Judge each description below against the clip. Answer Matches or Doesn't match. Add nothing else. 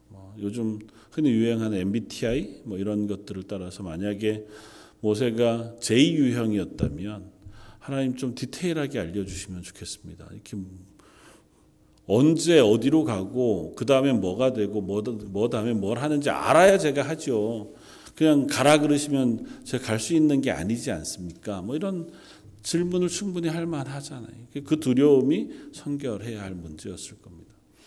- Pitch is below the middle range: Matches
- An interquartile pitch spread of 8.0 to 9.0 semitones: Doesn't match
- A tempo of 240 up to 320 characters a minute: Matches